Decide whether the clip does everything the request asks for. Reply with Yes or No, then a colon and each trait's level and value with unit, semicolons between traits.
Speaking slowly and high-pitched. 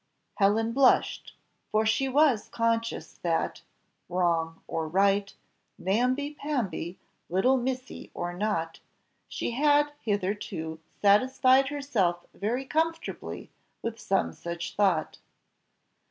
Yes: slow, 105 wpm; high, 215 Hz